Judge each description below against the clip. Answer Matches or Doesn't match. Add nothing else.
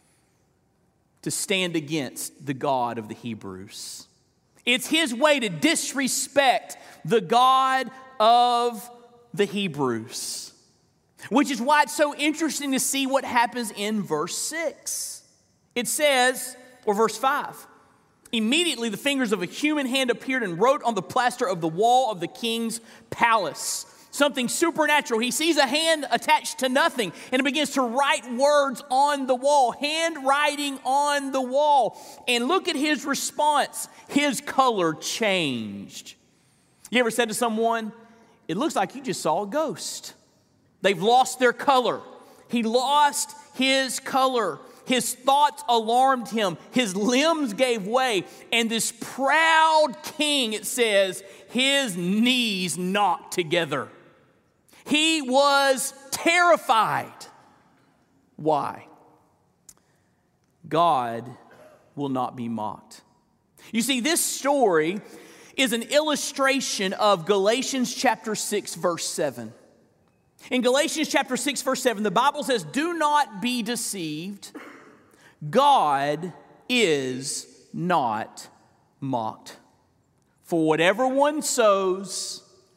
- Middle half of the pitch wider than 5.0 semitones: Matches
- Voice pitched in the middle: Doesn't match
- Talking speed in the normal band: Doesn't match